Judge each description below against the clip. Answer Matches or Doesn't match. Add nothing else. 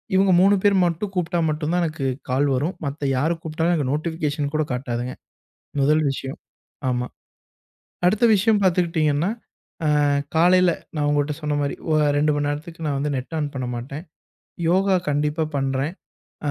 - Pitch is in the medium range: Matches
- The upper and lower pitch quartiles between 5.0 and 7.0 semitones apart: Doesn't match